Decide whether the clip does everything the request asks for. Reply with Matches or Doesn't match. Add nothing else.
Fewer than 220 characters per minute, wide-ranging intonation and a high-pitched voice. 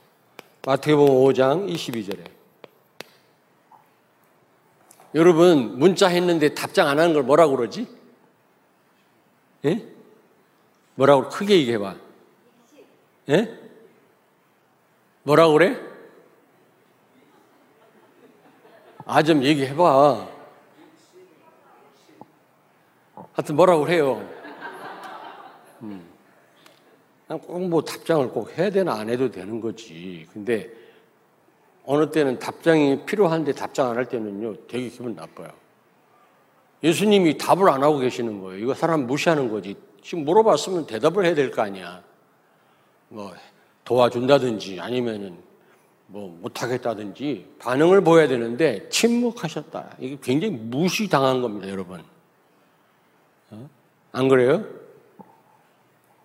Doesn't match